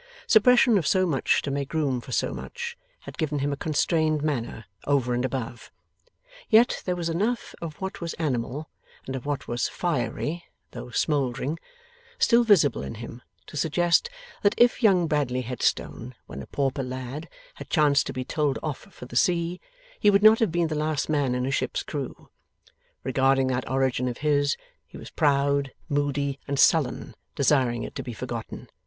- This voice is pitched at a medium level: Yes, medium, 145 Hz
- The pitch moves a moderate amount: Yes, average, 4.3 semitones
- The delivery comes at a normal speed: Yes, average, 180 wpm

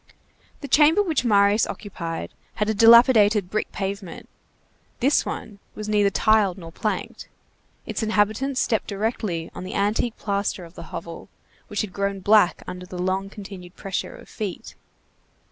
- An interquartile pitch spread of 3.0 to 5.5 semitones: No, narrow, 2.6 semitones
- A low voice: No, high, 205 Hz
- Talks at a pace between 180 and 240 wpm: No, average, 150 wpm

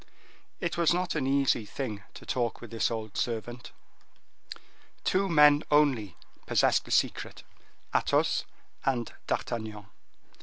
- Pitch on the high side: No, low, 125 Hz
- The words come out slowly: Yes, slow, 120 wpm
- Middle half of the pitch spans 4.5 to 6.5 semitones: Yes, average, 4.9 semitones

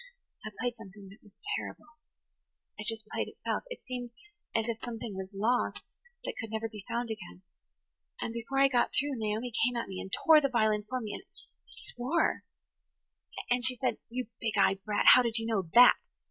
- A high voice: Yes, high, 230 Hz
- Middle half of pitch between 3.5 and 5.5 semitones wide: No, average, 2.8 semitones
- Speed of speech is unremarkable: Yes, average, 180 wpm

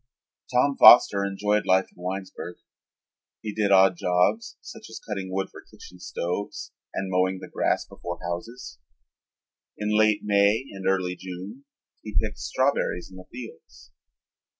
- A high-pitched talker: No, very low, 95 Hz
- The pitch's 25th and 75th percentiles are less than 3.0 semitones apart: Yes, narrow, 2.5 semitones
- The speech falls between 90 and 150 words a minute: Yes, average, 145 wpm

